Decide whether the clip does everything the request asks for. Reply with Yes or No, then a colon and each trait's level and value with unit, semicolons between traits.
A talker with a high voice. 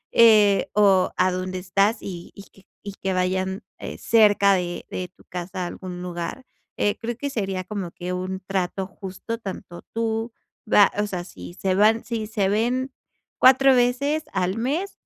Yes: high, 195 Hz